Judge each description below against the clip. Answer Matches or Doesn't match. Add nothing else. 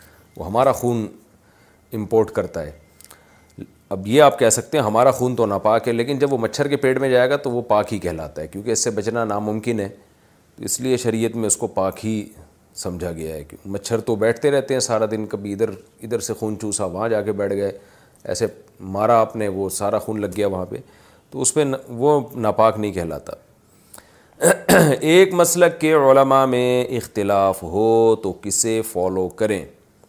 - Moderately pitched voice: Doesn't match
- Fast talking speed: Matches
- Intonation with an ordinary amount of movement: Matches